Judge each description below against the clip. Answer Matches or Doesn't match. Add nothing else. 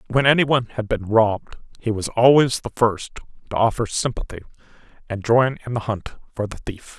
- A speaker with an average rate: Matches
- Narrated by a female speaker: Doesn't match